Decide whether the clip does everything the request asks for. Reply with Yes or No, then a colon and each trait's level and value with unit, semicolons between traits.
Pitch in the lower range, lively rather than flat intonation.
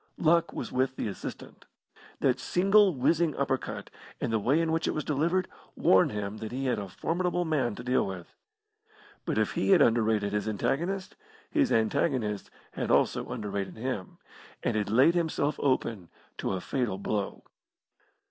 Yes: low, 130 Hz; wide, 7.6 semitones